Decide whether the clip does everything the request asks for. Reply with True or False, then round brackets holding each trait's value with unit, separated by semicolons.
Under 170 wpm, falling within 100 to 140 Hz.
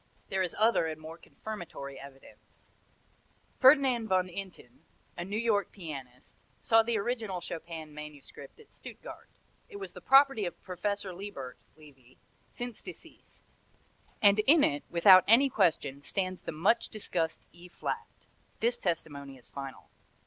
False (140 wpm; 185 Hz)